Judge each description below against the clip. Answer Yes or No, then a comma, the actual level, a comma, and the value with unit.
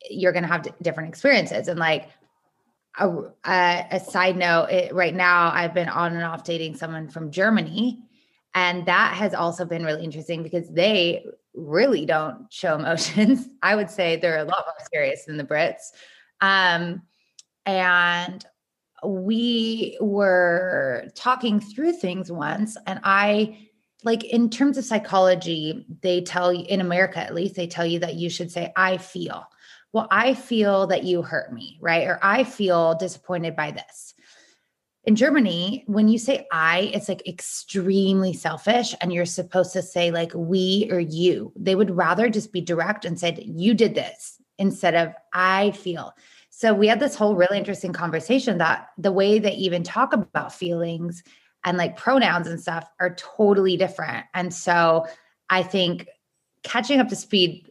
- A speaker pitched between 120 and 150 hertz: No, medium, 185 Hz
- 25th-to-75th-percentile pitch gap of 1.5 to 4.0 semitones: Yes, average, 3.6 semitones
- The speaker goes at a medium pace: Yes, average, 165 wpm